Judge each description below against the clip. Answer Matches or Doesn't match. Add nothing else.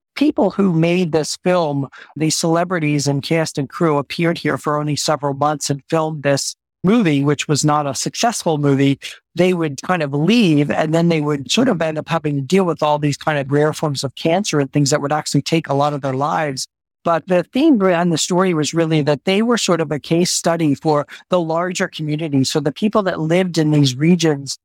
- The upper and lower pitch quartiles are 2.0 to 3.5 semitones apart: Matches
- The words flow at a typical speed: Doesn't match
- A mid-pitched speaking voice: Matches